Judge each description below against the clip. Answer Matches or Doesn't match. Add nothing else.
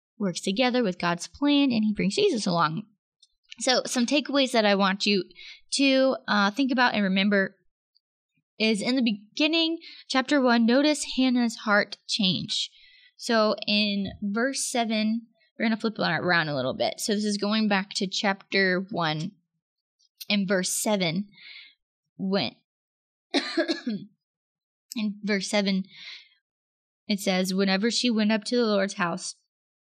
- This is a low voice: Doesn't match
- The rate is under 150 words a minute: Matches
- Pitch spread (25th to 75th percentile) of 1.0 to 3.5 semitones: Doesn't match